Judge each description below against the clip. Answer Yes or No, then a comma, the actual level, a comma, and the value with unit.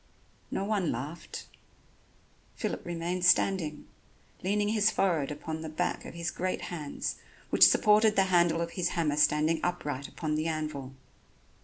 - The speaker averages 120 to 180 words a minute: Yes, average, 145 wpm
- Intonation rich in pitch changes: No, average, 3.4 semitones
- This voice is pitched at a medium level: Yes, medium, 170 Hz